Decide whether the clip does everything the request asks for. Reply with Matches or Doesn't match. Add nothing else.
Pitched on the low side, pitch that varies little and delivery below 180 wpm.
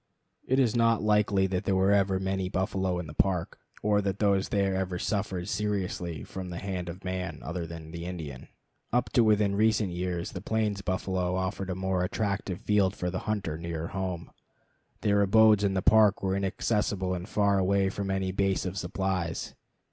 Doesn't match